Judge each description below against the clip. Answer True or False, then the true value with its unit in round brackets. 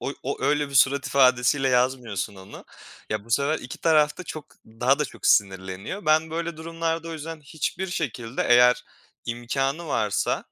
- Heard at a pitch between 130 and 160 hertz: True (140 Hz)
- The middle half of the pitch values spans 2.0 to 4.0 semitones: False (4.6 semitones)